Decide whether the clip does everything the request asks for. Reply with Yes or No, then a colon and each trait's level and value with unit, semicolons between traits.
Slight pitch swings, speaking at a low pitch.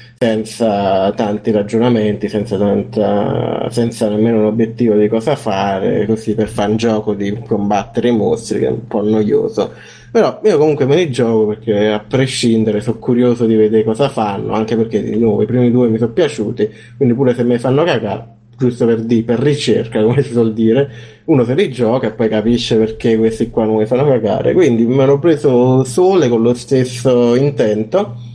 Yes: narrow, 2.2 semitones; low, 115 Hz